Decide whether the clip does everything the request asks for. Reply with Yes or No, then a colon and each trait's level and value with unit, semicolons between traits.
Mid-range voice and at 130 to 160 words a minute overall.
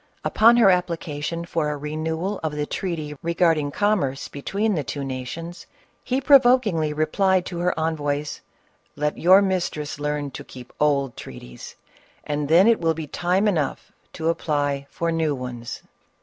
Yes: medium, 160 Hz; average, 155 wpm